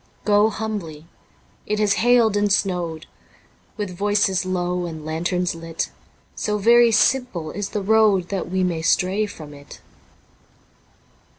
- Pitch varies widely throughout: No, average, 3.5 semitones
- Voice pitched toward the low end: No, high, 190 Hz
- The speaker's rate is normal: No, slow, 130 wpm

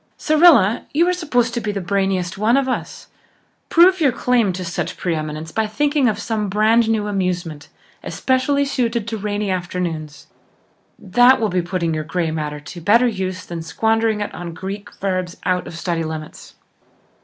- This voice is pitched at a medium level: No, high, 200 Hz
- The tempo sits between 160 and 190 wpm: Yes, average, 175 wpm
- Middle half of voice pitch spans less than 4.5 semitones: No, average, 5.0 semitones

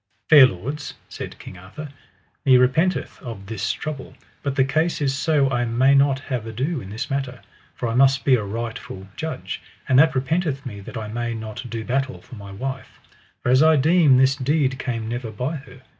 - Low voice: Yes, low, 130 Hz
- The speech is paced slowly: No, average, 200 wpm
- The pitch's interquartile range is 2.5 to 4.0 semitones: Yes, average, 3.3 semitones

